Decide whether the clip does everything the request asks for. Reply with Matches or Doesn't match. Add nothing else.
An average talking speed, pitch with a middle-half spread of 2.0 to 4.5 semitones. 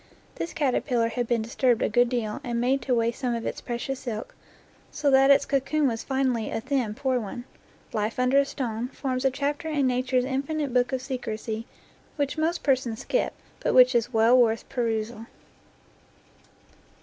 Matches